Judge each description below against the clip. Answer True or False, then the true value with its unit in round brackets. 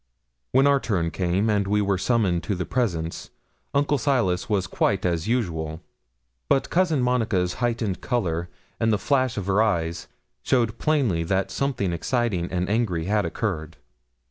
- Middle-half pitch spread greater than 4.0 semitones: True (5.5 semitones)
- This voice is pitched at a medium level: False (100 Hz)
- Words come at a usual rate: True (155 wpm)